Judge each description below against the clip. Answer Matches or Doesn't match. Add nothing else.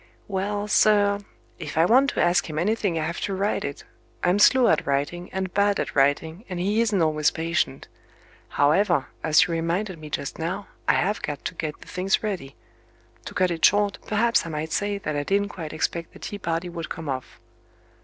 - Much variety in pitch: Doesn't match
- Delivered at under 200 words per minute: Doesn't match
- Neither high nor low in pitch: Matches